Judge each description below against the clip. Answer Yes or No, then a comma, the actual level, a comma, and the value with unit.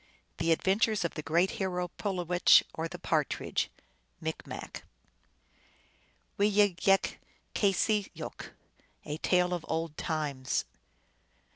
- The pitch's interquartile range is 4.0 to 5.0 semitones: No, average, 3.1 semitones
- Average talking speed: No, slow, 105 wpm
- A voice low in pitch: No, medium, 180 Hz